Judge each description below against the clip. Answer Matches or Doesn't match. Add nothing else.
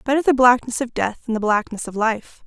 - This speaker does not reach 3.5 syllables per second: Doesn't match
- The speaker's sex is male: Doesn't match